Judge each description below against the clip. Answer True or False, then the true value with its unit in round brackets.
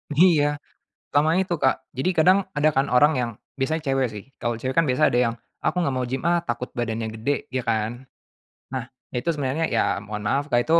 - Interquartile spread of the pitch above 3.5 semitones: True (4.5 semitones)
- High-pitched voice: False (135 Hz)